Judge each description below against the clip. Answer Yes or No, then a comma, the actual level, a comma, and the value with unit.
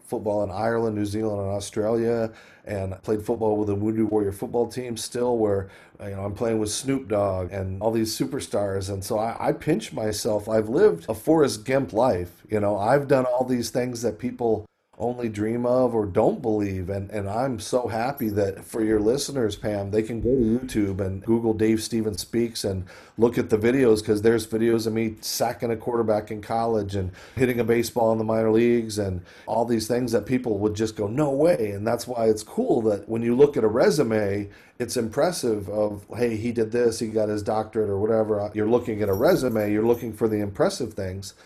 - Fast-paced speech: Yes, fast, 210 wpm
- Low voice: Yes, low, 110 Hz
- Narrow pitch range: Yes, narrow, 2.1 semitones